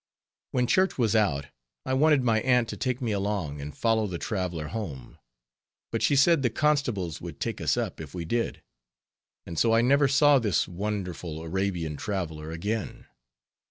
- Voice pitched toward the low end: Yes, low, 105 Hz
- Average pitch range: No, wide, 6.7 semitones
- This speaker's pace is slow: No, average, 170 wpm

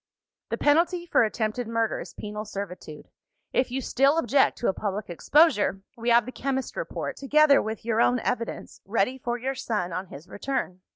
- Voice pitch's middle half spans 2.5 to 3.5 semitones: No, average, 4.4 semitones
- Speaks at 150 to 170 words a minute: No, average, 180 wpm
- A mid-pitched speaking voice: No, high, 235 Hz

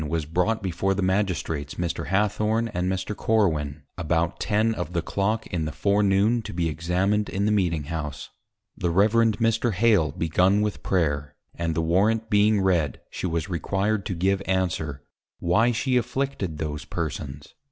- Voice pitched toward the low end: Yes, very low, 95 Hz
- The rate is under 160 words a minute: No, average, 165 wpm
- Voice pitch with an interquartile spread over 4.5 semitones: No, average, 4.2 semitones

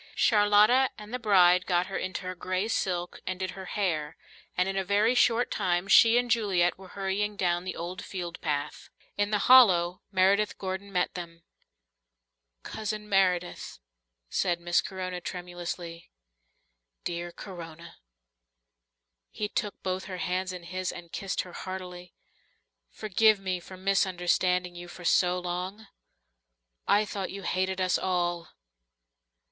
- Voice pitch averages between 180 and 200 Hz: Yes, medium, 185 Hz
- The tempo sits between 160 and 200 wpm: No, average, 140 wpm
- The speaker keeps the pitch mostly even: Yes, narrow, 2.2 semitones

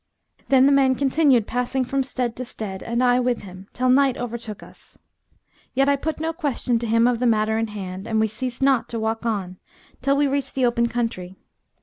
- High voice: Yes, high, 245 Hz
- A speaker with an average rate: No, fast, 215 wpm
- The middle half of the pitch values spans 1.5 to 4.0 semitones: Yes, average, 3.3 semitones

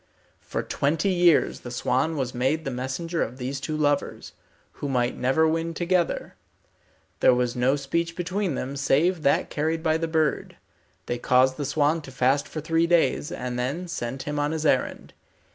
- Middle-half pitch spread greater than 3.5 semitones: Yes, average, 3.9 semitones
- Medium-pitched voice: Yes, medium, 145 Hz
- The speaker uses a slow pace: No, average, 180 wpm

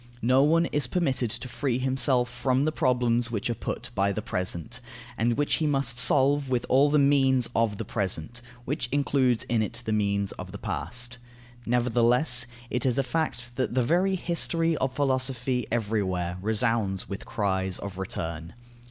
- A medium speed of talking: Yes, average, 170 wpm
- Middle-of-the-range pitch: No, low, 125 Hz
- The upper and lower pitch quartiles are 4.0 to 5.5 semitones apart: No, average, 3.6 semitones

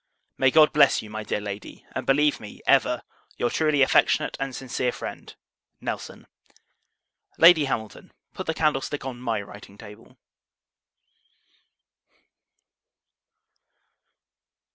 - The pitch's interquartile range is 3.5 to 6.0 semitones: Yes, average, 5.2 semitones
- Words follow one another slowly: Yes, slow, 110 wpm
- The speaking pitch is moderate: No, low, 130 Hz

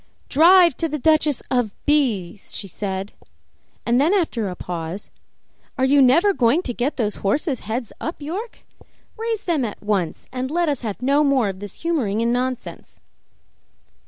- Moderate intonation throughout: No, wide, 6.7 semitones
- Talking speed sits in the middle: Yes, average, 170 wpm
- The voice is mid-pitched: No, very high, 255 Hz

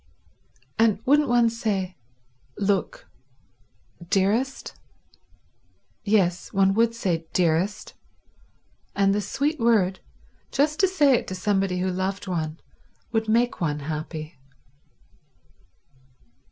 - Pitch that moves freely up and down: No, average, 4.3 semitones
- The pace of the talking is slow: Yes, slow, 100 wpm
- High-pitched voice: Yes, high, 195 Hz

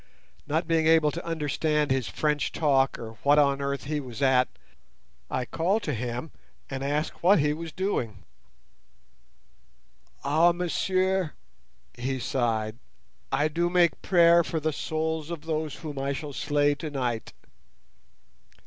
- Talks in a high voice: No, medium, 150 Hz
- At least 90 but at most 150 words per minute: Yes, average, 140 wpm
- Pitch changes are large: No, average, 3.4 semitones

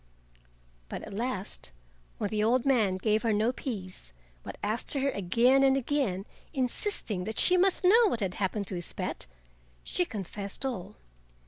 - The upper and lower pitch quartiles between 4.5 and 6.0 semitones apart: Yes, wide, 5.4 semitones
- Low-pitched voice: No, high, 220 Hz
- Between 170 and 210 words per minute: No, average, 160 wpm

